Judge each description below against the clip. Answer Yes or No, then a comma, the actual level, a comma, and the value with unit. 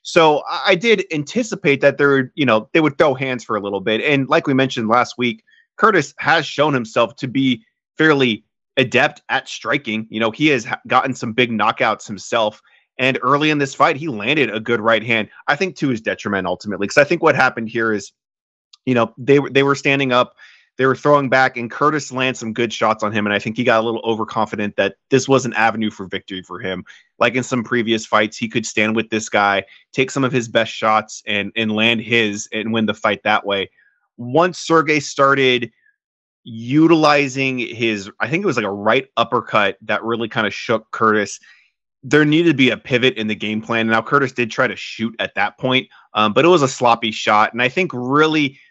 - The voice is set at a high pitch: No, low, 120 Hz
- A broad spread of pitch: No, average, 3.9 semitones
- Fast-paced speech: Yes, fast, 220 wpm